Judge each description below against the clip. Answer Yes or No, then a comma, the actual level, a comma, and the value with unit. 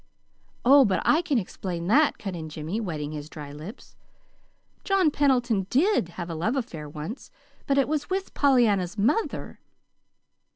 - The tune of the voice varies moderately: No, wide, 9.0 semitones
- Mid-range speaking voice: No, high, 215 Hz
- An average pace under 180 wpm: Yes, average, 155 wpm